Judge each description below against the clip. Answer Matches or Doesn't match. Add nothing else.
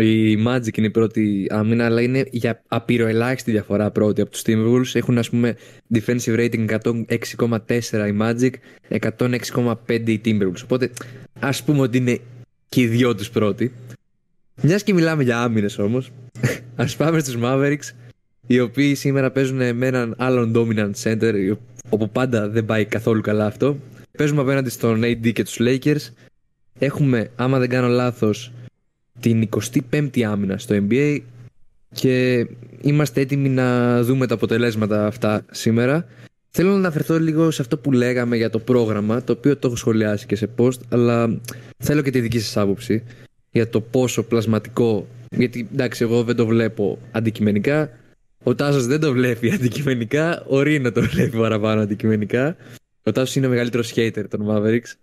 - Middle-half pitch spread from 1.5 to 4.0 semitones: Matches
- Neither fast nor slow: Matches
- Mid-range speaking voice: Doesn't match